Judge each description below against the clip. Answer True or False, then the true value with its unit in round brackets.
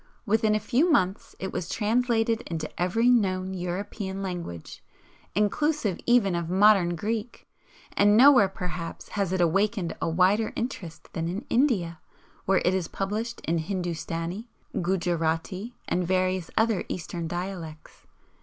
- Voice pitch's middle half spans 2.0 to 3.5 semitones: False (4.0 semitones)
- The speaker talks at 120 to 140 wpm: True (135 wpm)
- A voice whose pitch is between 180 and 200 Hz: True (190 Hz)